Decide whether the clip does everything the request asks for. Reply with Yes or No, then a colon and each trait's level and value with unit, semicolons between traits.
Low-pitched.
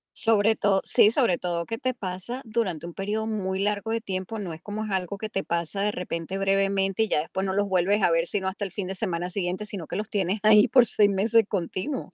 No: high, 195 Hz